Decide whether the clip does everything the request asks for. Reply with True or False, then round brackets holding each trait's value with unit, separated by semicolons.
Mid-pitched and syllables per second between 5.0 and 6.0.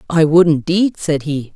False (160 Hz; 4.4 syllables/s)